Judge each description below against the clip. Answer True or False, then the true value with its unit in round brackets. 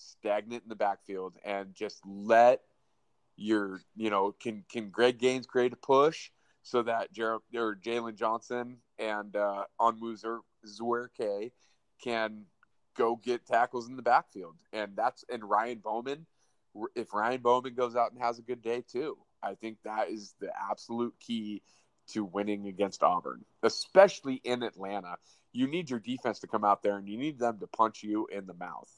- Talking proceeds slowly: False (170 wpm)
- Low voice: True (115 Hz)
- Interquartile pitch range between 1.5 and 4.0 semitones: True (2.9 semitones)